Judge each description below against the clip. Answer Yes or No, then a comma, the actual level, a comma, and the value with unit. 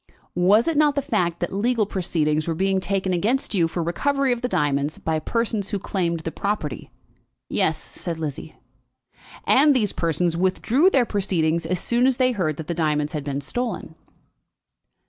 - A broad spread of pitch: Yes, wide, 6.2 semitones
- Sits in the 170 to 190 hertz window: Yes, medium, 185 Hz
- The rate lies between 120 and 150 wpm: No, average, 175 wpm